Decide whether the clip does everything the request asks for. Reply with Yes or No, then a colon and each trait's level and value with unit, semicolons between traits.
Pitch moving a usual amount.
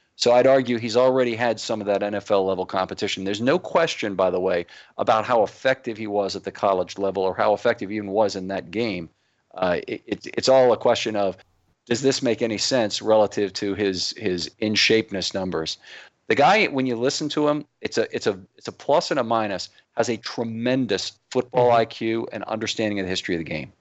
Yes: average, 3.8 semitones